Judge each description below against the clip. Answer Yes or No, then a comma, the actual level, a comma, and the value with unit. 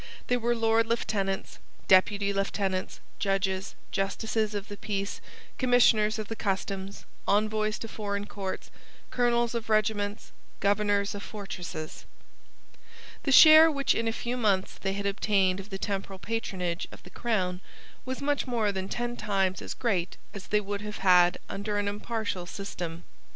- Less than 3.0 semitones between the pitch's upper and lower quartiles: Yes, narrow, 2.6 semitones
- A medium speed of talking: Yes, average, 150 wpm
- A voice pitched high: Yes, high, 205 Hz